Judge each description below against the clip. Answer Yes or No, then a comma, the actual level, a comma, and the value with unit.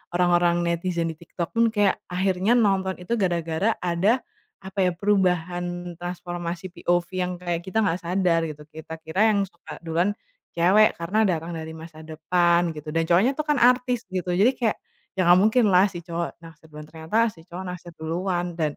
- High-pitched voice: No, medium, 175 Hz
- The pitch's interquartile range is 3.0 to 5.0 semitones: No, narrow, 2.5 semitones